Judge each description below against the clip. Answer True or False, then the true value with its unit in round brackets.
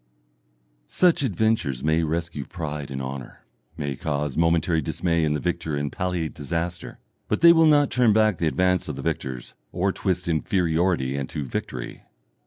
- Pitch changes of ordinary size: True (4.1 semitones)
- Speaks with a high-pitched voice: False (85 Hz)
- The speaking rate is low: False (160 wpm)